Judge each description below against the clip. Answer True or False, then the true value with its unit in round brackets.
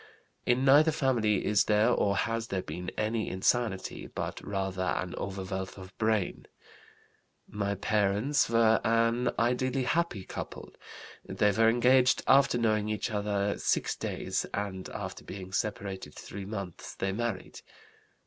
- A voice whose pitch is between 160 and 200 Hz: False (105 Hz)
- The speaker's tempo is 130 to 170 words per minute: True (135 wpm)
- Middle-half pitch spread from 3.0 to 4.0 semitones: True (3.3 semitones)